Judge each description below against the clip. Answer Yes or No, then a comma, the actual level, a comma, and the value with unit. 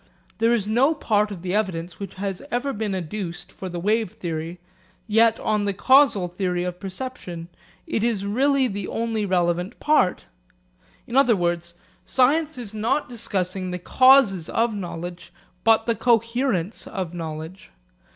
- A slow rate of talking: No, average, 150 wpm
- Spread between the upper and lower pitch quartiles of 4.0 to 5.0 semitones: Yes, average, 4.5 semitones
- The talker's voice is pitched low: No, high, 205 Hz